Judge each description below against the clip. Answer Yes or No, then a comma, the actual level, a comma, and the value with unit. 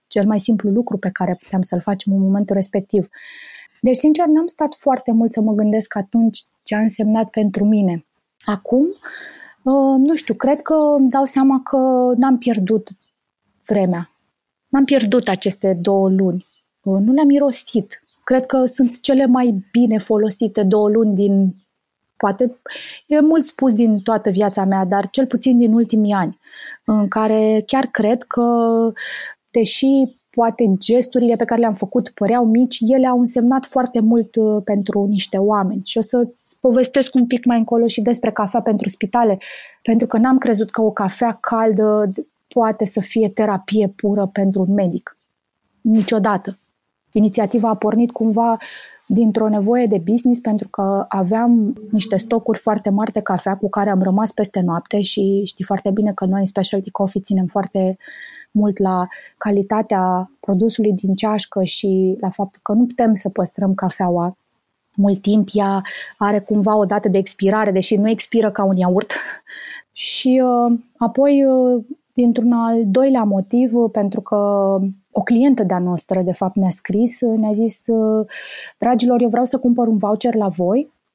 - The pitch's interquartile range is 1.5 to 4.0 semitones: Yes, average, 3.2 semitones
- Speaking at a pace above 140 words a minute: Yes, average, 160 wpm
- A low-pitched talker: No, high, 220 Hz